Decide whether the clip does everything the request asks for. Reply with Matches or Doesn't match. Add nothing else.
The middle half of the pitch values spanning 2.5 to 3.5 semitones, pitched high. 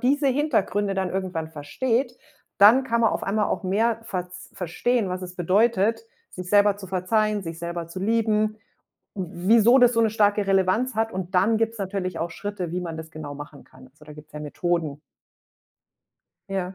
Doesn't match